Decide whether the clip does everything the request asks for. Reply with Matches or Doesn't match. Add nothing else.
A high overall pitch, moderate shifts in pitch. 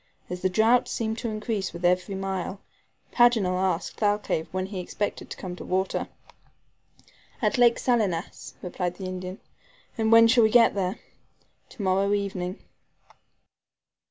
Matches